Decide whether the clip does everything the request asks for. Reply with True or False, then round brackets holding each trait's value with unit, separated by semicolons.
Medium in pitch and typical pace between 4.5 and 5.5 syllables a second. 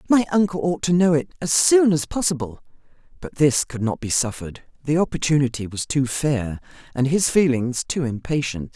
True (145 Hz; 5.2 syllables/s)